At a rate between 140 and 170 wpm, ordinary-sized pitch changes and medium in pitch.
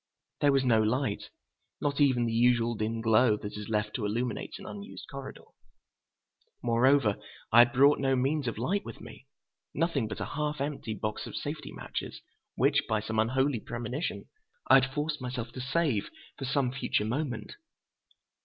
No: average, 165 wpm; average, 3.8 semitones; low, 125 Hz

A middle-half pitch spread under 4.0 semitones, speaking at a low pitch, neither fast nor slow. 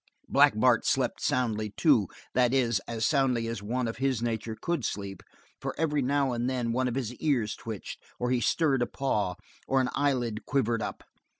Yes: average, 3.1 semitones; low, 120 Hz; average, 190 wpm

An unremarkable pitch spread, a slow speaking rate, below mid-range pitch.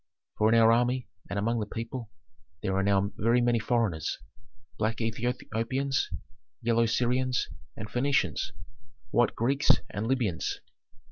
No: narrow, 2.3 semitones; slow, 130 wpm; low, 115 Hz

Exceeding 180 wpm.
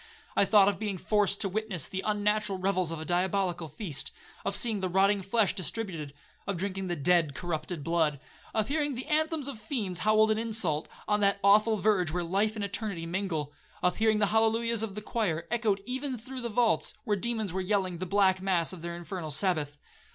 Yes: average, 190 wpm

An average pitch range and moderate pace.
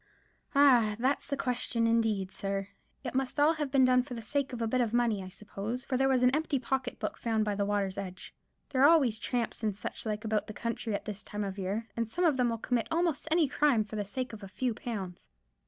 No: average, 4.0 semitones; fast, 250 wpm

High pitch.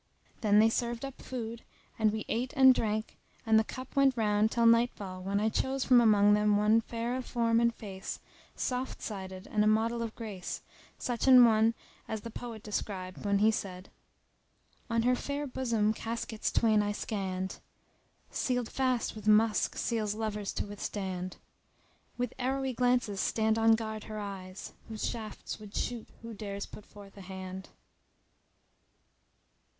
Yes: high, 220 Hz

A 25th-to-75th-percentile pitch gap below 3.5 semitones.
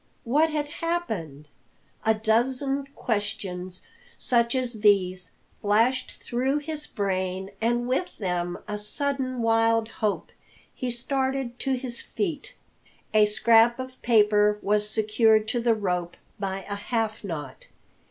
No: average, 4.0 semitones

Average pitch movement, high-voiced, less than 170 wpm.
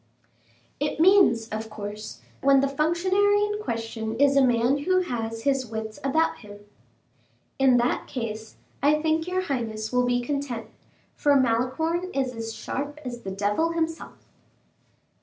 No: wide, 5.8 semitones; very high, 265 Hz; average, 145 wpm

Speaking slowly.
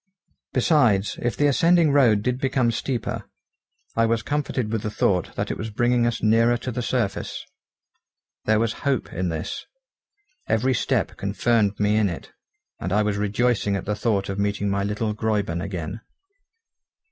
No: average, 165 wpm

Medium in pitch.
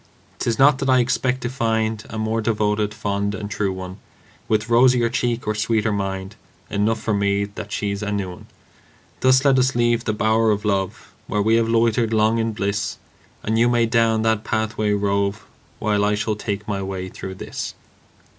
No: low, 110 Hz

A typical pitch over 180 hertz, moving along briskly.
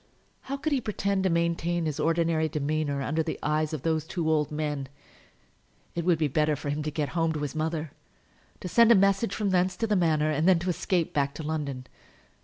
No: medium, 160 Hz; fast, 215 wpm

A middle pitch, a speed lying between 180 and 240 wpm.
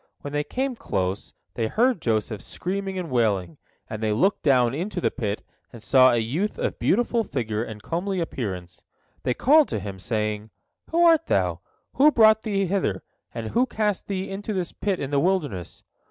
Yes: medium, 145 Hz; average, 185 wpm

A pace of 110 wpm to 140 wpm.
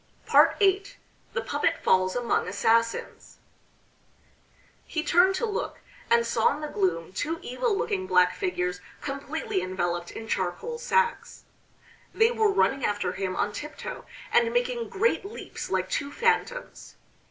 Yes: slow, 135 wpm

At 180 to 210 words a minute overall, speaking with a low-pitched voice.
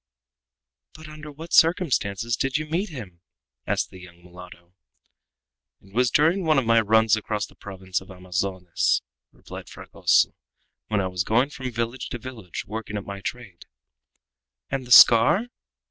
No: average, 155 wpm; low, 115 Hz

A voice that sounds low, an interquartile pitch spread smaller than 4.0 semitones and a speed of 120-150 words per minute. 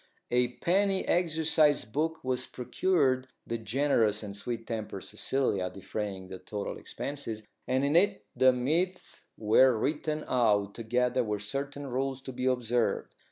No: low, 125 Hz; average, 4.8 semitones; average, 140 wpm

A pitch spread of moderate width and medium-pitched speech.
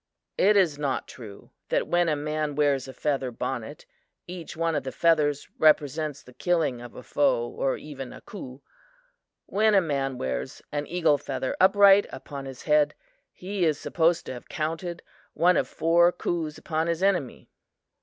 Yes: average, 4.1 semitones; medium, 150 Hz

